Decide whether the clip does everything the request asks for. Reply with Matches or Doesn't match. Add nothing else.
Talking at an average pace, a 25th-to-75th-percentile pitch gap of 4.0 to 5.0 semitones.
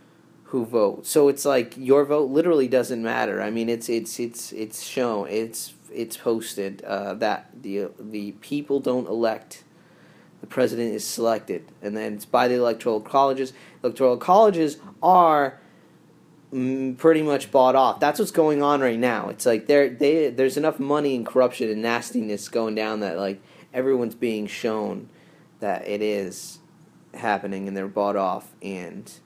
Matches